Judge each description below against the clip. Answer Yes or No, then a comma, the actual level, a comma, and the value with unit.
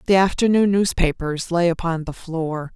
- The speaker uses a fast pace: No, average, 150 wpm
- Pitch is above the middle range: No, medium, 175 Hz